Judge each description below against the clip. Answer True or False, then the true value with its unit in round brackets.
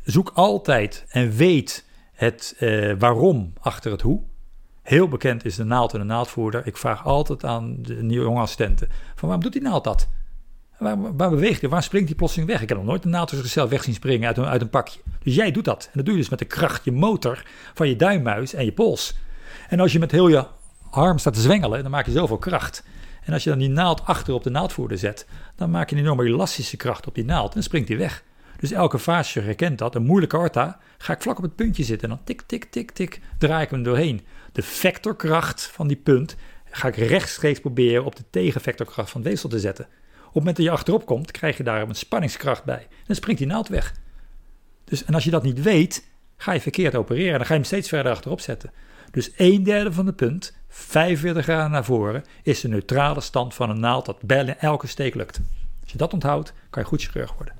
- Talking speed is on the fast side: True (235 wpm)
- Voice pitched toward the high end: False (140 Hz)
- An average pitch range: False (5.9 semitones)